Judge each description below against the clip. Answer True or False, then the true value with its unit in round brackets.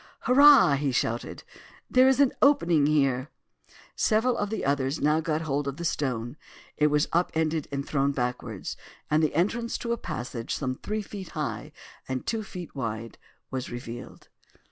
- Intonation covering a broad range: True (6.4 semitones)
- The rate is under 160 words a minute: False (165 wpm)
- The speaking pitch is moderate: True (150 Hz)